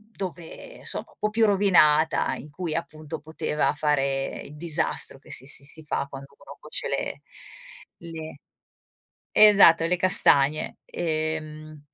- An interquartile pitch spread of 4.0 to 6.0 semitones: No, narrow, 2.4 semitones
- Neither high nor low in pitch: Yes, medium, 155 Hz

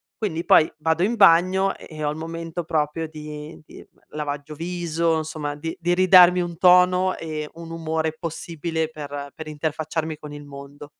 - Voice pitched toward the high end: No, medium, 160 Hz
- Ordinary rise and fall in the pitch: No, narrow, 2.1 semitones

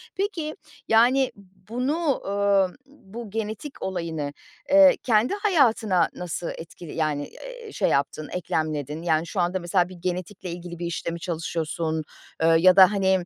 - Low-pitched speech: No, medium, 185 Hz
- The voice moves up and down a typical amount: No, wide, 5.8 semitones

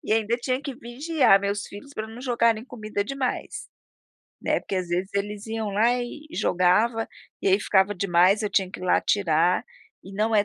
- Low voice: No, high, 210 Hz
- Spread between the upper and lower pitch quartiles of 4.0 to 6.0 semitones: No, average, 3.4 semitones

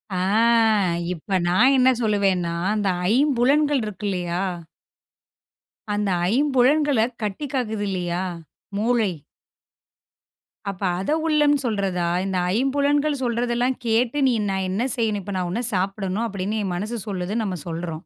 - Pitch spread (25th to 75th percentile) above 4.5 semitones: Yes, average, 5.1 semitones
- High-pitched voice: Yes, high, 215 Hz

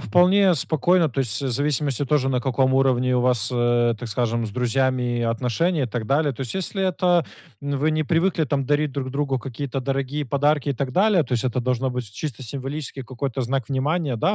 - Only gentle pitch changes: No, average, 3.3 semitones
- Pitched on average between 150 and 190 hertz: No, low, 135 Hz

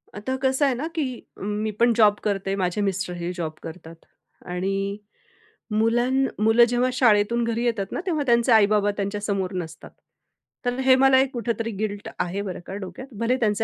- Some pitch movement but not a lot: Yes, average, 3.6 semitones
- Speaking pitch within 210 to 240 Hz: Yes, high, 215 Hz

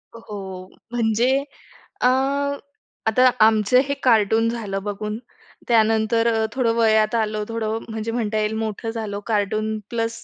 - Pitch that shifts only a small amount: Yes, narrow, 1.5 semitones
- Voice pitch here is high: Yes, high, 220 Hz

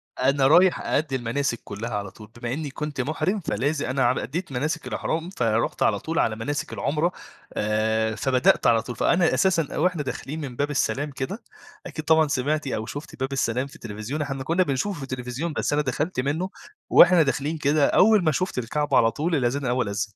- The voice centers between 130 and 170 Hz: Yes, medium, 140 Hz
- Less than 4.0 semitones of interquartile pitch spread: No, average, 4.3 semitones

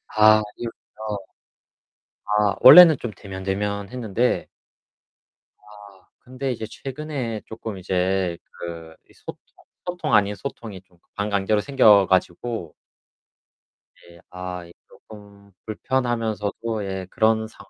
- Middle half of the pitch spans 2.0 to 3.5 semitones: Yes, average, 3.1 semitones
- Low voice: Yes, low, 105 Hz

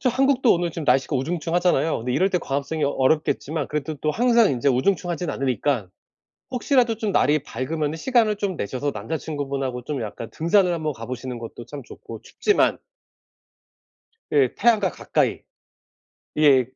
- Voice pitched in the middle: Yes, medium, 150 Hz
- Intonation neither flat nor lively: No, wide, 5.7 semitones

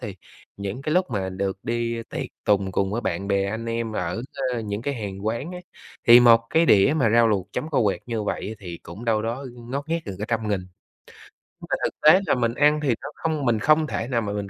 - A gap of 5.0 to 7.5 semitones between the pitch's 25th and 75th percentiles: No, average, 4.1 semitones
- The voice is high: No, low, 115 Hz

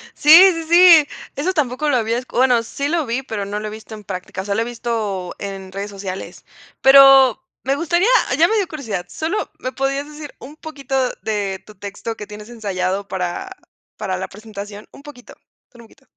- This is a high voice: Yes, high, 230 Hz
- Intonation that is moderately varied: No, wide, 5.8 semitones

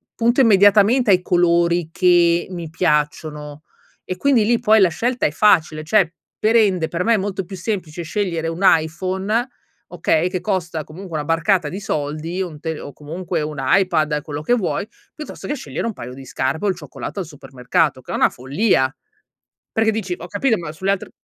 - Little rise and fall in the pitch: No, average, 4.5 semitones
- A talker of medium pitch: Yes, medium, 175 Hz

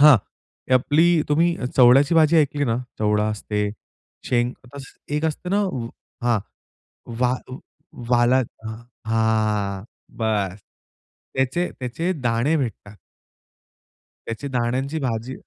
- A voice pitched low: Yes, low, 125 Hz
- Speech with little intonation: No, average, 4.2 semitones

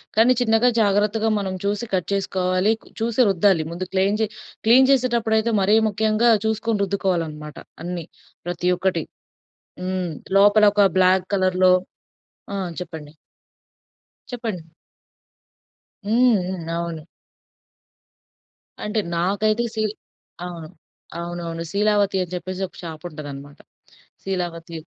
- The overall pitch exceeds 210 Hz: No, high, 190 Hz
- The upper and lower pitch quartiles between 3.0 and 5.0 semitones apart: Yes, average, 3.7 semitones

